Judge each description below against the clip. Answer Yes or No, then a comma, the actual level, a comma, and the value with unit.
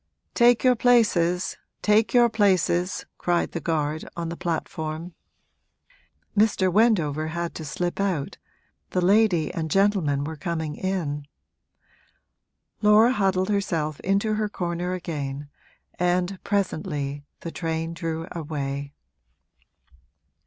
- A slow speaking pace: Yes, slow, 110 wpm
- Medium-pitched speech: Yes, medium, 175 Hz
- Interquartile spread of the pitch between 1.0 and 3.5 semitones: No, average, 4.0 semitones